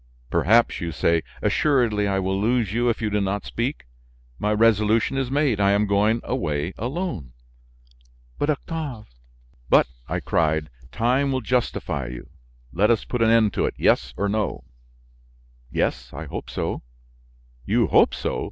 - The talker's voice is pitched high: No, low, 105 Hz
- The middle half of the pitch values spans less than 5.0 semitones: No, wide, 5.5 semitones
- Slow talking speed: No, average, 160 wpm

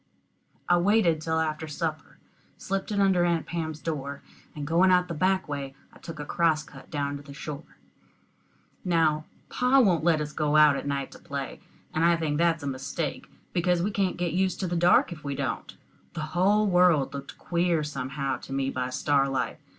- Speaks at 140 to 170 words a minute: No, average, 195 wpm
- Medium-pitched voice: Yes, medium, 160 Hz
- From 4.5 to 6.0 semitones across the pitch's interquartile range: No, average, 3.6 semitones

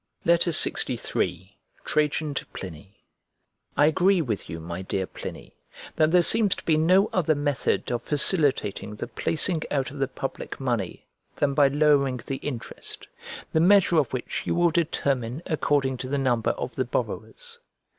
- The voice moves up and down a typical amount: Yes, average, 4.7 semitones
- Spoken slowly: No, average, 155 wpm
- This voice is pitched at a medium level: Yes, medium, 145 Hz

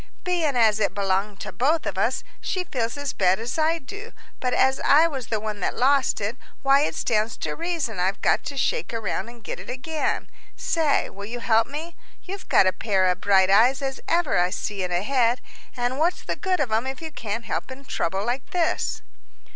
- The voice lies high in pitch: Yes, high, 245 Hz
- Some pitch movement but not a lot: No, wide, 5.8 semitones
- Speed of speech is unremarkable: No, fast, 220 wpm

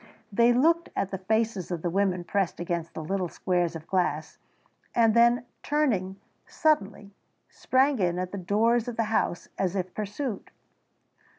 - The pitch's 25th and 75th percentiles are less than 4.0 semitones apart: No, average, 4.5 semitones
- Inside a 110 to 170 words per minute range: Yes, average, 160 wpm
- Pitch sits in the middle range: No, high, 200 Hz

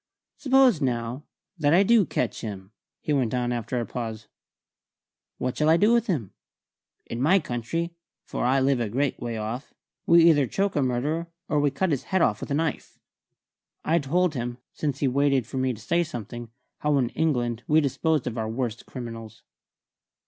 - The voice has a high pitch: No, low, 135 Hz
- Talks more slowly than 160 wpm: No, average, 185 wpm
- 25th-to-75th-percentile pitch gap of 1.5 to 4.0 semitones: No, average, 5.0 semitones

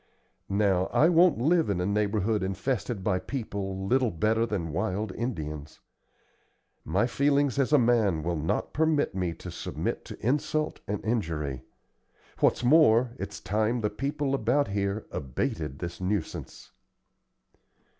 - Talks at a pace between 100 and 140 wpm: Yes, slow, 135 wpm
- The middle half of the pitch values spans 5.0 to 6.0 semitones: Yes, wide, 5.6 semitones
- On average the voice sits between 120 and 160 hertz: No, low, 105 Hz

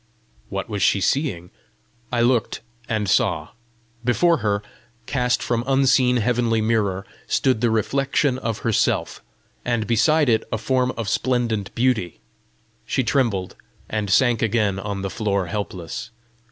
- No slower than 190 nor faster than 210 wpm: No, slow, 135 wpm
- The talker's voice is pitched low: Yes, low, 115 Hz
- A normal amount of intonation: Yes, average, 3.6 semitones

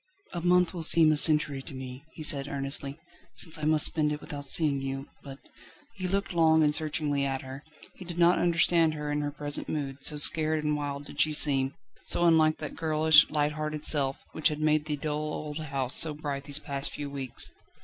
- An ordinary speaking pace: No, fast, 215 wpm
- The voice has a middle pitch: Yes, medium, 150 Hz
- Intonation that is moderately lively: No, narrow, 2.0 semitones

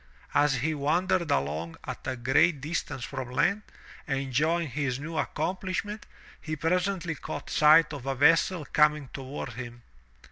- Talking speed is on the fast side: No, average, 140 wpm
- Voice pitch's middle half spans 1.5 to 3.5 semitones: No, average, 4.0 semitones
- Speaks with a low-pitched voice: No, medium, 150 Hz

